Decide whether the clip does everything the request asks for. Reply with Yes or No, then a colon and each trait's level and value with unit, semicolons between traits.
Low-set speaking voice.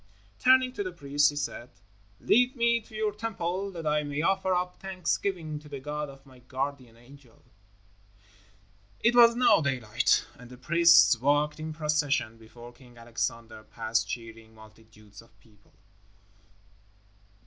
No: medium, 145 Hz